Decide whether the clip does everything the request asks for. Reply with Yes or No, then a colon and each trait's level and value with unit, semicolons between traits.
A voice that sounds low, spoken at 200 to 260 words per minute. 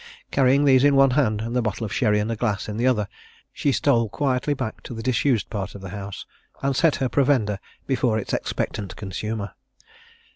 Yes: low, 115 Hz; fast, 205 wpm